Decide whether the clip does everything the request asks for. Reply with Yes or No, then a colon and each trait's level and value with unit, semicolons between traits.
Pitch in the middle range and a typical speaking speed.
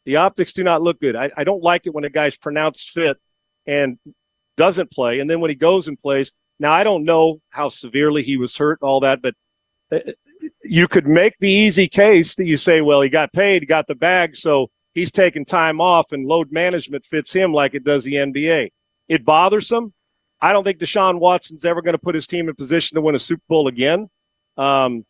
No: medium, 160 Hz; fast, 225 wpm